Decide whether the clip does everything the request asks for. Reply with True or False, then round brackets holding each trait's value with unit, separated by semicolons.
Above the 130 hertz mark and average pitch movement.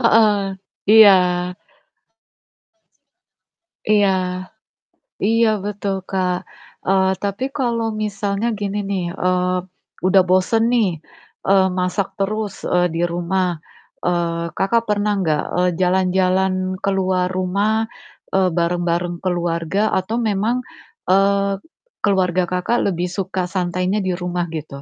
False (190 Hz; 2.2 semitones)